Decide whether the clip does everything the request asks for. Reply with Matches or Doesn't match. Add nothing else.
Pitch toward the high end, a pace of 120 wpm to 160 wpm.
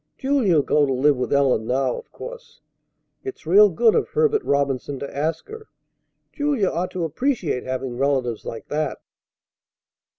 Doesn't match